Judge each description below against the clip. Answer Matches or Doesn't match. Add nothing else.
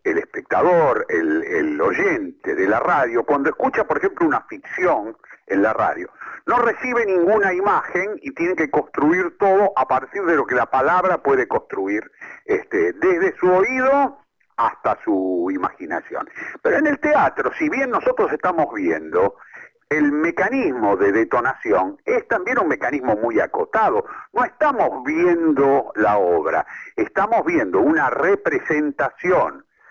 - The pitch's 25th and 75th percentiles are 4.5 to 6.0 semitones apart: Matches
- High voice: Matches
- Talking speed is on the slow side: Doesn't match